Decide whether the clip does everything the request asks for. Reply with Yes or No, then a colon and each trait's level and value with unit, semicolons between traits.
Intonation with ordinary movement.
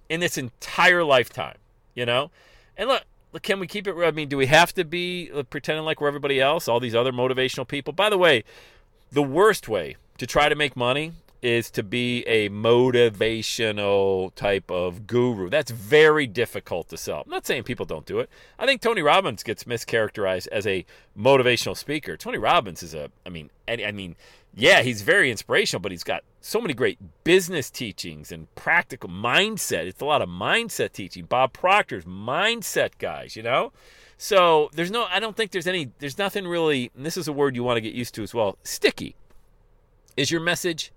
No: wide, 6.2 semitones